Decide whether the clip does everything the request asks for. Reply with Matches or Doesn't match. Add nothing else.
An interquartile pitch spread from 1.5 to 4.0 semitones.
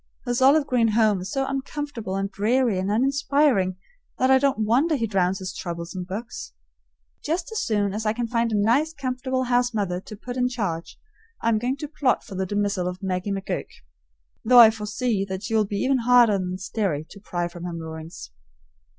Doesn't match